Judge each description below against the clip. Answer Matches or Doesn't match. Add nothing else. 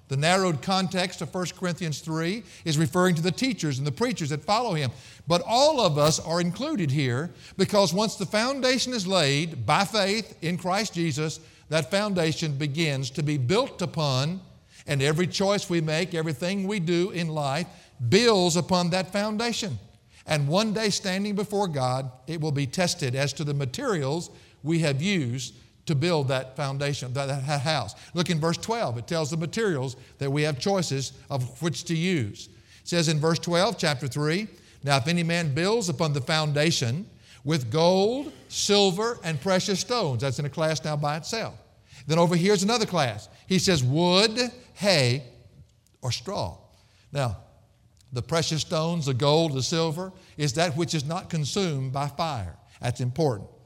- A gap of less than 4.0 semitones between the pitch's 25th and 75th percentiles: Doesn't match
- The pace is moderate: Matches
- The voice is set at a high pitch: Doesn't match